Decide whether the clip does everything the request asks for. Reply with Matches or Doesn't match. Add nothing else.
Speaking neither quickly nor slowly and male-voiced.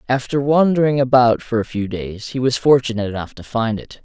Doesn't match